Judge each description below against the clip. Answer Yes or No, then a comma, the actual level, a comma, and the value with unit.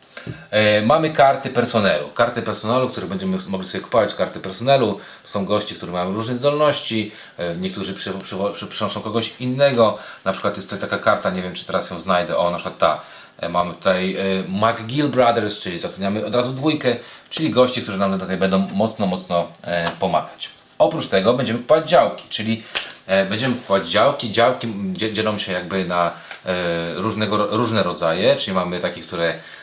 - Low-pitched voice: Yes, low, 110 Hz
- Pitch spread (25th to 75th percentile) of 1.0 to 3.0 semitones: No, average, 4.3 semitones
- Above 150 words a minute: Yes, fast, 160 wpm